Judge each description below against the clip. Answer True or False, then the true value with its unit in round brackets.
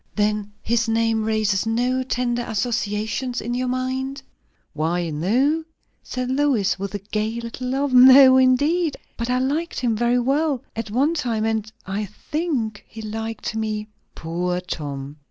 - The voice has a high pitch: True (230 Hz)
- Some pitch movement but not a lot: True (3.5 semitones)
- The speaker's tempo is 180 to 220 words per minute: False (150 wpm)